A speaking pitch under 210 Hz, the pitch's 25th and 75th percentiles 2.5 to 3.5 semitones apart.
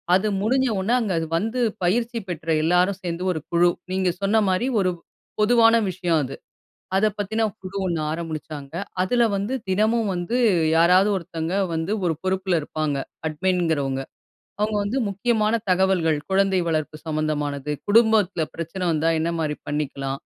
No: medium, 185 Hz; average, 4.6 semitones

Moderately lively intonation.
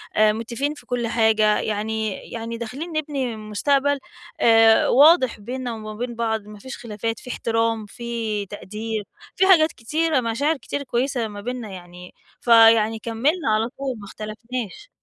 Yes: average, 3.1 semitones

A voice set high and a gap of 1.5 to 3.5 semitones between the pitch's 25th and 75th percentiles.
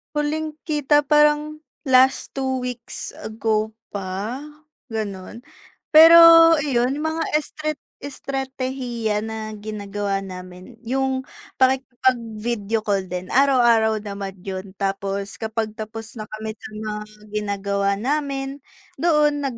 No: high, 235 Hz; average, 4.8 semitones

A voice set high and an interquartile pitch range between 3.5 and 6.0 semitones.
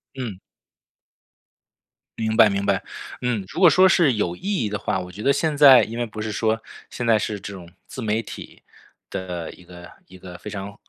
No: low, 110 Hz; average, 4.2 semitones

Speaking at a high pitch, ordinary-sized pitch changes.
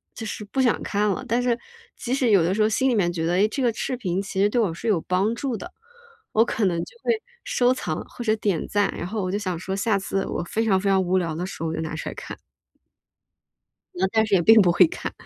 Yes: high, 200 Hz; average, 3.7 semitones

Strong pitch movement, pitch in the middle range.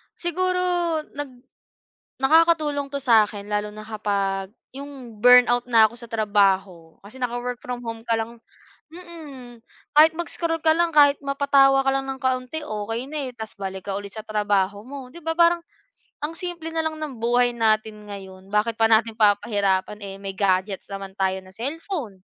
No: wide, 5.8 semitones; high, 235 Hz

